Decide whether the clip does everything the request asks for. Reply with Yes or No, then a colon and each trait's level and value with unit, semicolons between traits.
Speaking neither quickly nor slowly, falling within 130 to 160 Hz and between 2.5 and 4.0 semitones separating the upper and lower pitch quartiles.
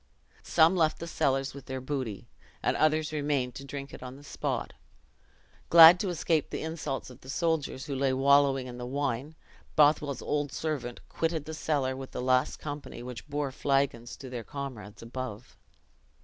Yes: average, 175 wpm; medium, 140 Hz; average, 2.8 semitones